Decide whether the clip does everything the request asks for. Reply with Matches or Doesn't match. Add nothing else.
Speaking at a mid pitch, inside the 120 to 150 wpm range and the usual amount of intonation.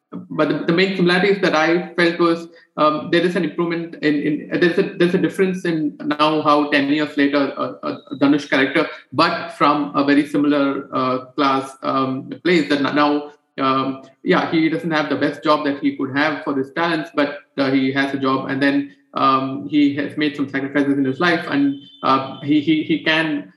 Doesn't match